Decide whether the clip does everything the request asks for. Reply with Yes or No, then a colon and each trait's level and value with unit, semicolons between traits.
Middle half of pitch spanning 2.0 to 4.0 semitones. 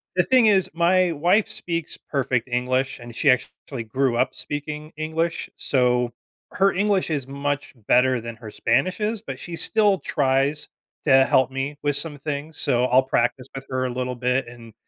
No: average, 4.4 semitones